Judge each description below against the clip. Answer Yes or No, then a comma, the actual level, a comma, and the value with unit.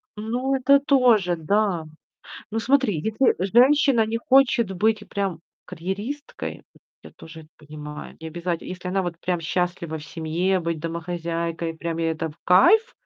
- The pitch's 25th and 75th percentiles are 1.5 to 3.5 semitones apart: No, wide, 5.6 semitones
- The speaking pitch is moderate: Yes, medium, 180 Hz